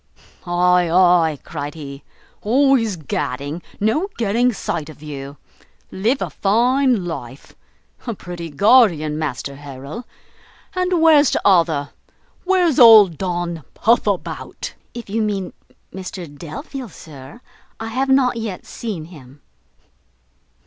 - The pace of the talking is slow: Yes, slow, 115 wpm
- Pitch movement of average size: No, wide, 7.2 semitones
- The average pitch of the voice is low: No, medium, 185 Hz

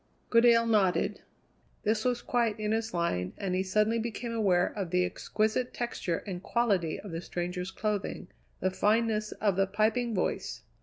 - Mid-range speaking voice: No, high, 210 Hz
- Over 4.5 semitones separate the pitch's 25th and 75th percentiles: No, average, 4.0 semitones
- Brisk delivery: No, average, 160 wpm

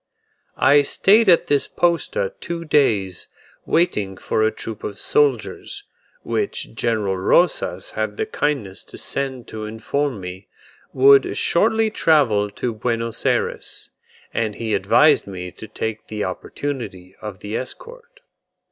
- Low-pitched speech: Yes, low, 120 Hz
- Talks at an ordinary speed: No, slow, 130 wpm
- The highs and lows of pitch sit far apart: Yes, wide, 8.3 semitones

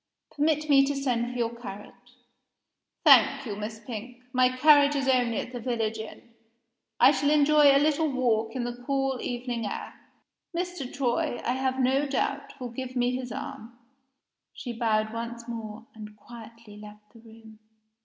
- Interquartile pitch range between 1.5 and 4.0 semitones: Yes, average, 3.1 semitones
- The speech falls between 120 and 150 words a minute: No, average, 165 wpm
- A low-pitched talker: No, high, 245 Hz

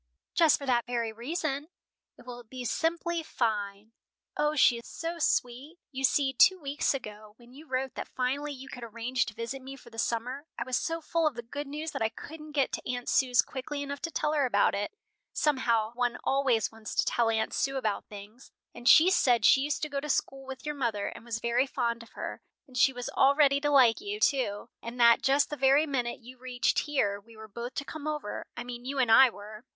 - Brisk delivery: Yes, fast, 230 wpm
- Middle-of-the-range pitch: No, very high, 255 Hz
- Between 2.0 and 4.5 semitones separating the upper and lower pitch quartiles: Yes, average, 3.5 semitones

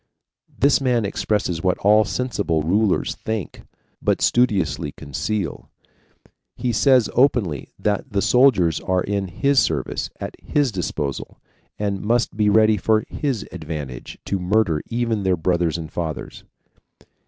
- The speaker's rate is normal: No, slow, 130 wpm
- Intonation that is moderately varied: Yes, average, 4.9 semitones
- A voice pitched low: Yes, low, 100 Hz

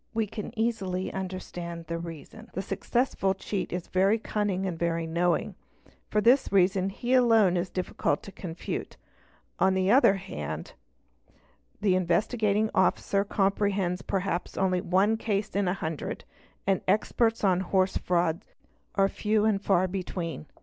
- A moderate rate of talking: Yes, average, 145 wpm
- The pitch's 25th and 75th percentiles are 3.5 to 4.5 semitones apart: No, narrow, 2.6 semitones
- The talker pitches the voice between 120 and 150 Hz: No, high, 190 Hz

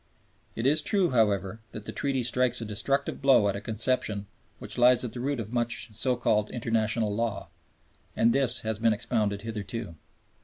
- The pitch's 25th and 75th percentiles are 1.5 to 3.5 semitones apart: Yes, average, 2.8 semitones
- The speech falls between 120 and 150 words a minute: No, average, 185 wpm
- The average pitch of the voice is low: Yes, low, 115 Hz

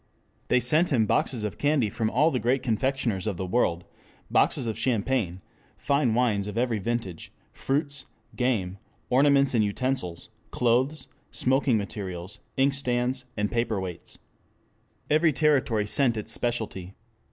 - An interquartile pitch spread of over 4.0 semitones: Yes, average, 4.4 semitones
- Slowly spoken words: Yes, slow, 130 wpm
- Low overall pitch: Yes, low, 120 Hz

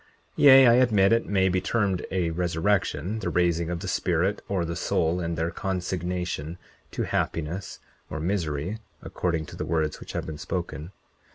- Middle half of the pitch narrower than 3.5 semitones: Yes, average, 2.9 semitones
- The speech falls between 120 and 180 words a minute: Yes, average, 170 wpm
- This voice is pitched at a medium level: No, very low, 90 Hz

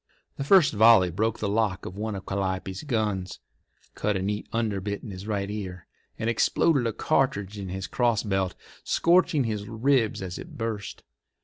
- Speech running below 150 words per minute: No, average, 170 wpm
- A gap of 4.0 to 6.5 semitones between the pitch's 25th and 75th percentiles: No, average, 3.0 semitones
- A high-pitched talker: No, low, 105 Hz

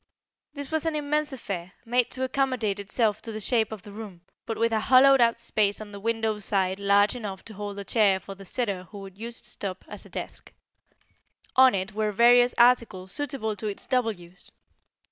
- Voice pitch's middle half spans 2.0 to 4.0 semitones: Yes, average, 3.6 semitones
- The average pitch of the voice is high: Yes, high, 220 Hz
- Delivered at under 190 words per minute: No, fast, 205 wpm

